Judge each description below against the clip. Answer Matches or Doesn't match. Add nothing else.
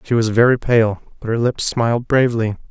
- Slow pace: Doesn't match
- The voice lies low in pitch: Matches